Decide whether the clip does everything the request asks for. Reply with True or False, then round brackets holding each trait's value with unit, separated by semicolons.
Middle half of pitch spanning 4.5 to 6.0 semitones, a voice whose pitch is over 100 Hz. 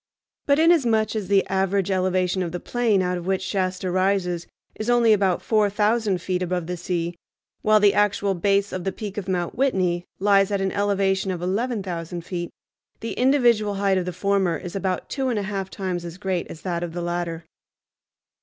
False (2.5 semitones; 190 Hz)